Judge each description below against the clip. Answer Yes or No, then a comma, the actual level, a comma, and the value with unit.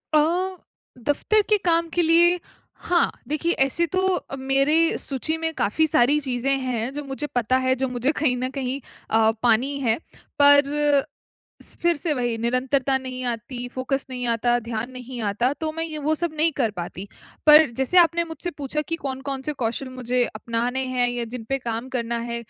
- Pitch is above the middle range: Yes, very high, 265 Hz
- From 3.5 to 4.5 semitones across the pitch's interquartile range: Yes, average, 3.9 semitones